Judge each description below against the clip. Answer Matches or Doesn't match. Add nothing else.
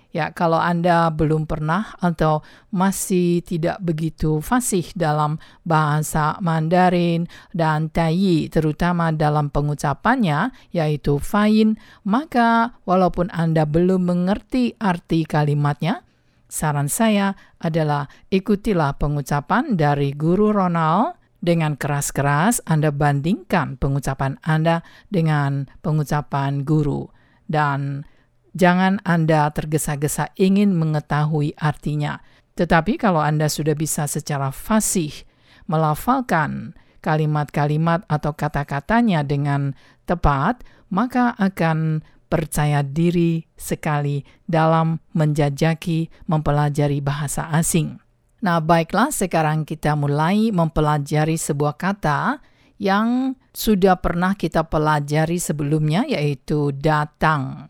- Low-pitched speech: Doesn't match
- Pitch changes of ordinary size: Matches